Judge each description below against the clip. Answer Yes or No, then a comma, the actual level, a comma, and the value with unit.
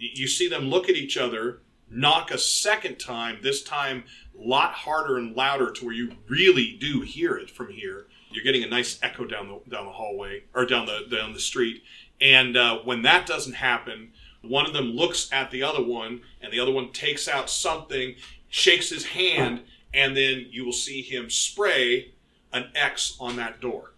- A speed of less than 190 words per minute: No, average, 200 wpm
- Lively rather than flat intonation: Yes, wide, 7.0 semitones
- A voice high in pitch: No, low, 135 Hz